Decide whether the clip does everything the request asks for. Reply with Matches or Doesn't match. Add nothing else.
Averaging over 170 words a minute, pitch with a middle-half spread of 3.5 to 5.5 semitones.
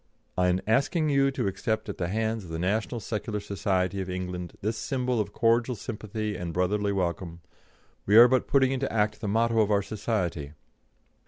Matches